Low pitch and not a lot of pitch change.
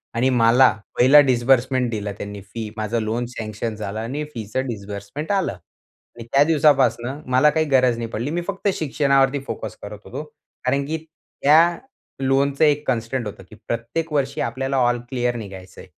No: low, 125 Hz; average, 3.7 semitones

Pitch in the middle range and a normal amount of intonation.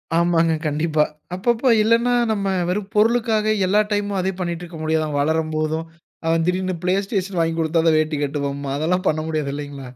Yes: medium, 165 Hz; average, 4.1 semitones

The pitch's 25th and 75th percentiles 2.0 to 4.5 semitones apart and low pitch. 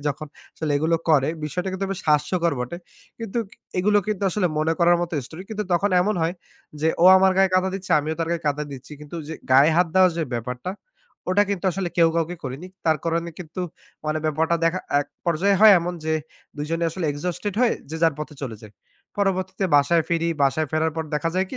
No: average, 3.4 semitones; medium, 170 Hz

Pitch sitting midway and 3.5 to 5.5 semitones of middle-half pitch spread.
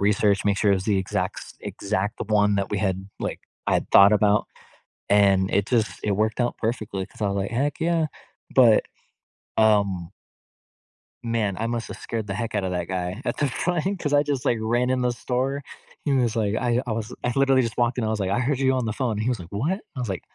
No: low, 110 Hz; average, 3.9 semitones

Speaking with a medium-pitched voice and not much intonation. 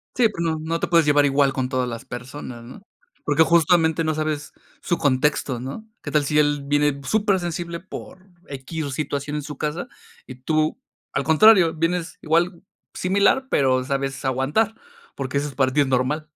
No: medium, 150 Hz; average, 3.6 semitones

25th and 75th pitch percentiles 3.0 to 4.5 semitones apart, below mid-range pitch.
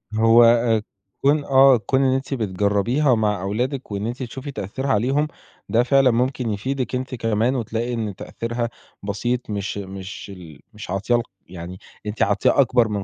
Yes: average, 4.0 semitones; low, 115 Hz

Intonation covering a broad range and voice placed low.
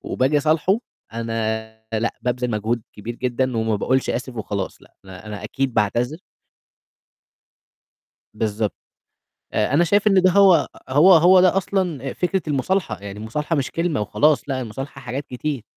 Yes: wide, 6.4 semitones; low, 130 Hz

